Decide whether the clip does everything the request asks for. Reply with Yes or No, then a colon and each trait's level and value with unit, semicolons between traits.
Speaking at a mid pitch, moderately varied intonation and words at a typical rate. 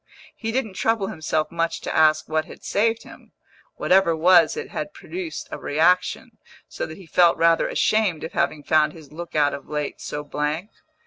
Yes: medium, 165 Hz; average, 3.9 semitones; average, 190 wpm